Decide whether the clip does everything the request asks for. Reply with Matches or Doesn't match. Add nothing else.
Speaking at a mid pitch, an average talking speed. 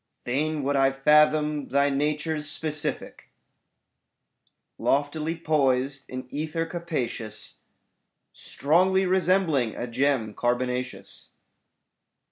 Doesn't match